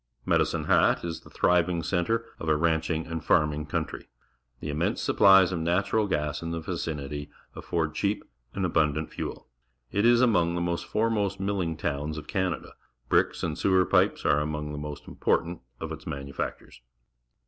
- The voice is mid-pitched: No, very low, 85 Hz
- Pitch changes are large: No, average, 3.6 semitones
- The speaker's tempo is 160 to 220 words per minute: Yes, average, 170 wpm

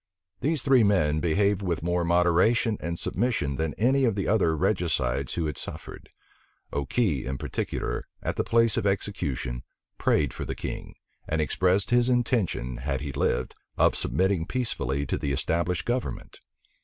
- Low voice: Yes, very low, 85 Hz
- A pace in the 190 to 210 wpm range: No, average, 155 wpm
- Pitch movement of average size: No, wide, 7.2 semitones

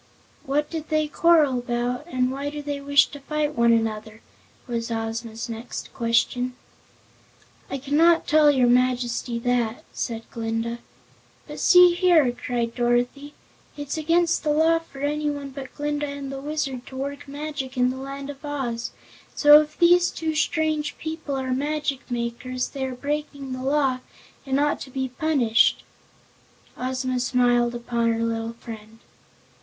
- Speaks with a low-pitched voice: No, very high, 270 Hz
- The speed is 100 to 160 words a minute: Yes, average, 150 wpm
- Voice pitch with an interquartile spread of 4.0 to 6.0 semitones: No, average, 3.5 semitones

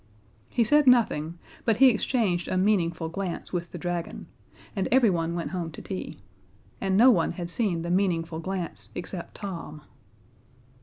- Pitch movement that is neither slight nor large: Yes, average, 3.9 semitones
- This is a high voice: No, medium, 180 Hz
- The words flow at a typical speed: Yes, average, 155 wpm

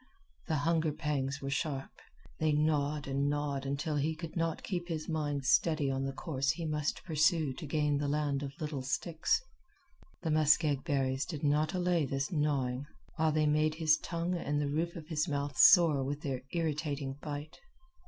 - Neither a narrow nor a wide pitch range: No, narrow, 2.1 semitones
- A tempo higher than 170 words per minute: Yes, average, 180 wpm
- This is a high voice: No, medium, 150 Hz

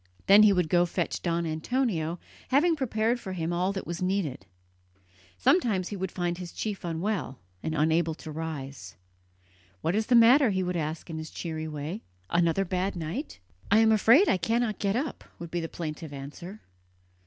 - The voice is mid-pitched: Yes, medium, 180 Hz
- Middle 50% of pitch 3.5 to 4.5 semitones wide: No, average, 4.9 semitones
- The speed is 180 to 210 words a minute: Yes, average, 185 wpm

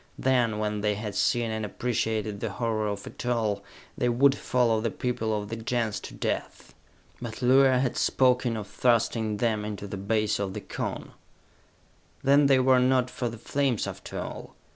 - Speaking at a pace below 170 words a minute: No, average, 180 wpm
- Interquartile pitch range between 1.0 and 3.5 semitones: Yes, average, 2.8 semitones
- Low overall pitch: Yes, low, 115 Hz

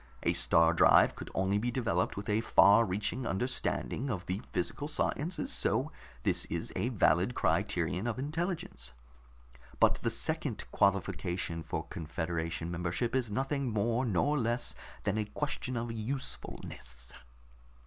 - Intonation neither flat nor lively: No, wide, 6.4 semitones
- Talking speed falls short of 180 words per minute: Yes, average, 140 wpm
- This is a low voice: Yes, low, 105 Hz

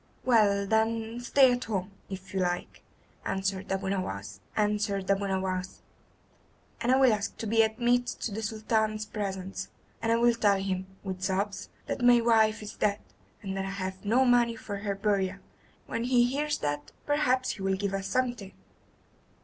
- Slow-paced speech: No, average, 160 wpm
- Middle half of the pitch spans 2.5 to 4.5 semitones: Yes, average, 3.2 semitones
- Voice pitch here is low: No, high, 210 Hz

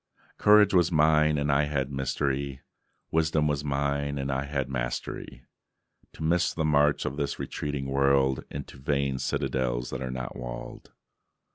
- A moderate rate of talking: Yes, average, 150 wpm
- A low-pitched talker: Yes, very low, 70 Hz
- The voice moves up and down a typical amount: No, narrow, 1.9 semitones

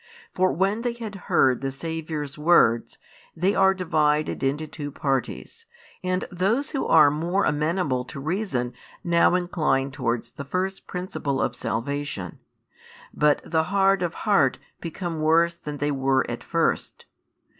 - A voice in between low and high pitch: Yes, medium, 160 Hz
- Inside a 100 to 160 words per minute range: Yes, average, 145 wpm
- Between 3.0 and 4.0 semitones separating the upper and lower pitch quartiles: No, average, 4.7 semitones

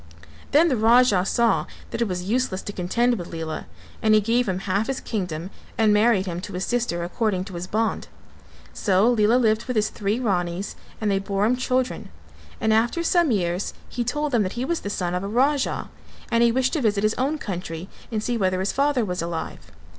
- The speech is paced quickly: Yes, fast, 215 wpm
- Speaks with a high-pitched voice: Yes, high, 215 Hz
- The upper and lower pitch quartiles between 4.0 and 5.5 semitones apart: Yes, average, 4.6 semitones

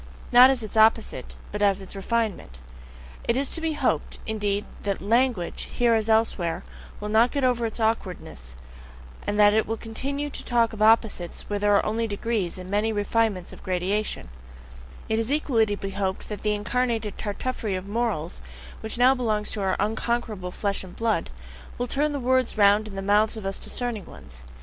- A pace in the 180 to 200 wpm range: Yes, average, 190 wpm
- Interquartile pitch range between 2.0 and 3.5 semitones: Yes, average, 2.7 semitones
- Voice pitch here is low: No, high, 215 Hz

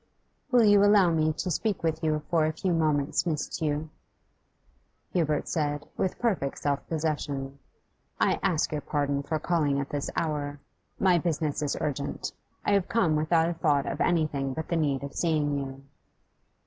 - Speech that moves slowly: No, average, 170 wpm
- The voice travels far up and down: No, average, 2.8 semitones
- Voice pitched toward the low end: No, medium, 155 Hz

